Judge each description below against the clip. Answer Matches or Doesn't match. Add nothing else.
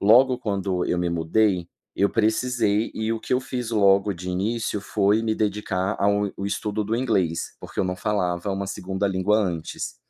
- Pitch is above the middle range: Doesn't match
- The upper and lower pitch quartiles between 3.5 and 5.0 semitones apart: Doesn't match